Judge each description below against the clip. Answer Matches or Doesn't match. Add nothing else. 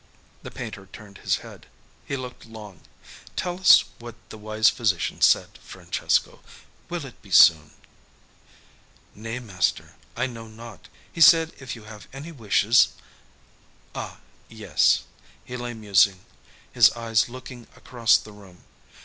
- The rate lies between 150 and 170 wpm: Doesn't match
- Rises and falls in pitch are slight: Doesn't match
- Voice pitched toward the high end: Doesn't match